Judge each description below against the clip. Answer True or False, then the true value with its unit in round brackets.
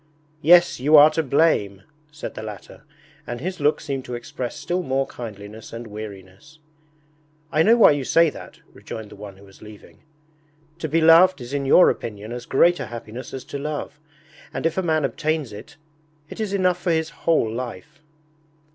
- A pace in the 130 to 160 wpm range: False (185 wpm)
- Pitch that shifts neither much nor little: False (6.5 semitones)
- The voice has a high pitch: False (140 Hz)